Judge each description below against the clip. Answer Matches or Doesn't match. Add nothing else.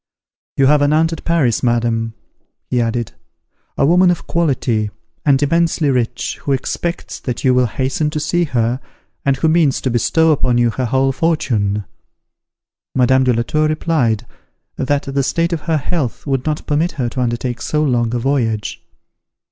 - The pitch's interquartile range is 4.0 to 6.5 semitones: Matches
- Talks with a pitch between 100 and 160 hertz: Matches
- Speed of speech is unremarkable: Matches